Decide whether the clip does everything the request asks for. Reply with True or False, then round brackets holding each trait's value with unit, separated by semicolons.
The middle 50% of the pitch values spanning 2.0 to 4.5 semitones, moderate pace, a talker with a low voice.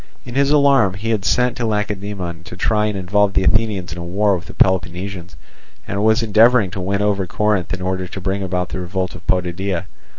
False (2.7 semitones; 210 wpm; 95 Hz)